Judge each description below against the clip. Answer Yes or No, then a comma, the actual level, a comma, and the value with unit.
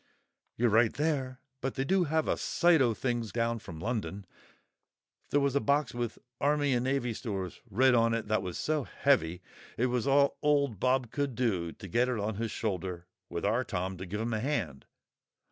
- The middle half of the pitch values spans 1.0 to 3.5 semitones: No, average, 4.8 semitones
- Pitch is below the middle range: Yes, low, 120 Hz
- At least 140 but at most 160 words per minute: No, average, 195 wpm